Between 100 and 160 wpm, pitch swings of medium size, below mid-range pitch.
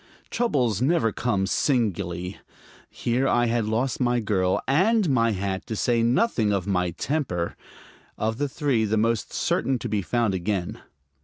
Yes: average, 155 wpm; average, 4.5 semitones; low, 115 Hz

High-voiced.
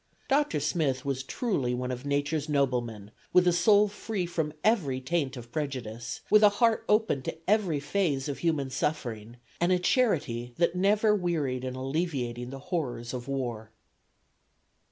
No: medium, 145 Hz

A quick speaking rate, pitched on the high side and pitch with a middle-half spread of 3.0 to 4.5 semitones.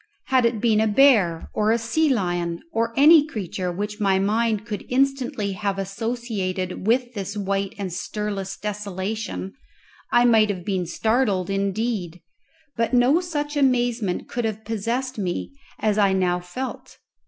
No: average, 150 wpm; high, 210 Hz; average, 3.8 semitones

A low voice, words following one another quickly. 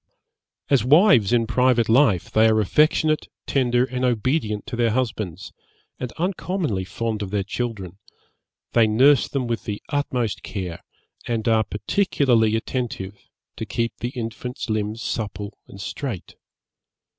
No: low, 115 Hz; slow, 135 wpm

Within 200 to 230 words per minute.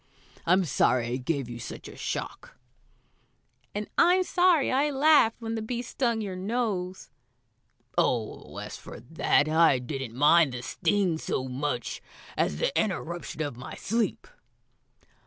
No: average, 140 wpm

